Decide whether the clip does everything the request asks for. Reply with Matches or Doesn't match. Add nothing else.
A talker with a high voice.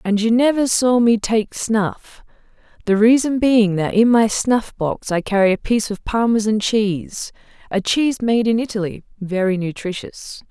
Matches